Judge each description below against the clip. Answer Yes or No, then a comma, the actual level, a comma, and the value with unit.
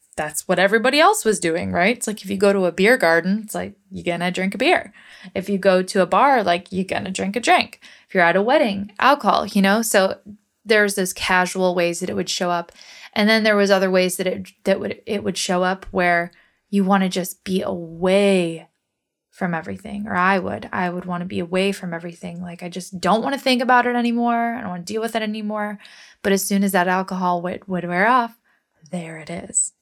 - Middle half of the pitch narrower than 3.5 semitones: Yes, average, 2.8 semitones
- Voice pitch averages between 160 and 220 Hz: Yes, high, 190 Hz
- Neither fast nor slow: No, fast, 235 wpm